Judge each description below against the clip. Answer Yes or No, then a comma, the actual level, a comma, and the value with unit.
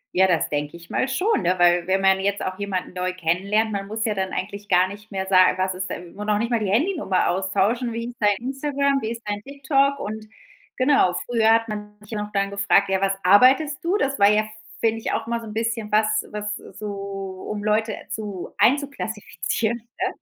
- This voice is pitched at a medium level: No, high, 210 Hz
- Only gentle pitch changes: No, average, 3.3 semitones